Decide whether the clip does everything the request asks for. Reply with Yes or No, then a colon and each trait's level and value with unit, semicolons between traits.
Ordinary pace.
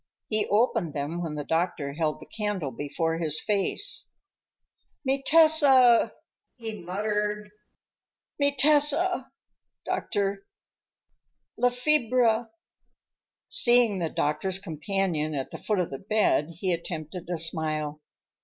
No: slow, 115 wpm